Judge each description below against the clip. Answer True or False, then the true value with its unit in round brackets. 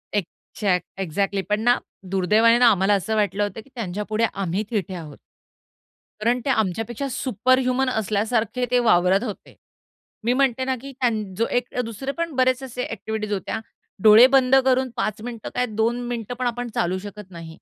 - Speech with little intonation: False (3.7 semitones)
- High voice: True (220 Hz)